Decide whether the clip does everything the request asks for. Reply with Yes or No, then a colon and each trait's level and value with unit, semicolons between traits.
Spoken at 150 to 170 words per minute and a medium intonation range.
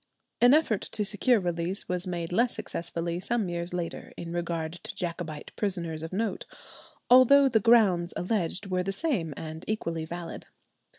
Yes: average, 160 wpm; average, 4.4 semitones